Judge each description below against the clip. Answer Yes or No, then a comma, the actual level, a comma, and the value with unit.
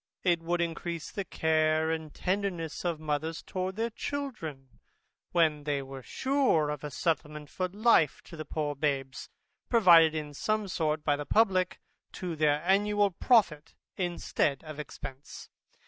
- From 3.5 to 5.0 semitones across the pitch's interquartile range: Yes, average, 3.8 semitones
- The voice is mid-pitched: Yes, medium, 160 Hz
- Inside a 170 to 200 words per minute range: No, average, 145 wpm